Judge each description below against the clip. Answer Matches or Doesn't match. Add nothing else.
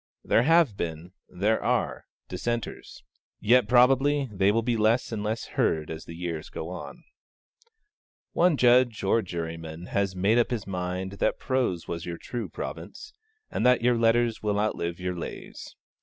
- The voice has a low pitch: Matches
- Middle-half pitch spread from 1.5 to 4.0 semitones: Doesn't match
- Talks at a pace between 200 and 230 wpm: Doesn't match